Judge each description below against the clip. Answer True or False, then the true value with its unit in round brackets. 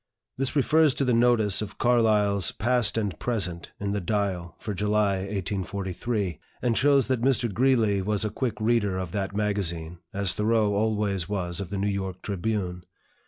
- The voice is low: True (105 Hz)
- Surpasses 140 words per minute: True (165 wpm)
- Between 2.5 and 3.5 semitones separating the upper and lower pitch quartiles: True (3.0 semitones)